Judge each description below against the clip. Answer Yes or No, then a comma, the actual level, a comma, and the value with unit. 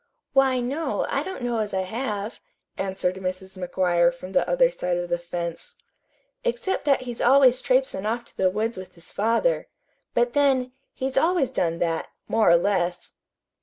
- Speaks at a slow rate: No, average, 170 wpm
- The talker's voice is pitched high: Yes, high, 220 Hz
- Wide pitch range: Yes, wide, 6.2 semitones